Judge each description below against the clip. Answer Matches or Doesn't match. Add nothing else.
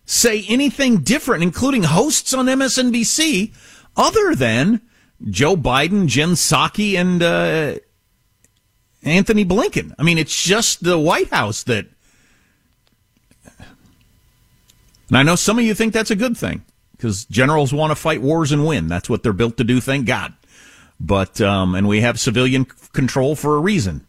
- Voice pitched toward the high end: Doesn't match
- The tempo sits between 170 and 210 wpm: Doesn't match